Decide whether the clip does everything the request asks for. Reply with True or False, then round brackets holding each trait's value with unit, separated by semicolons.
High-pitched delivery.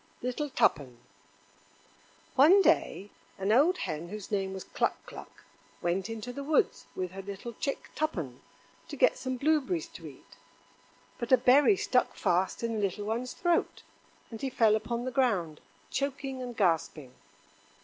True (235 Hz)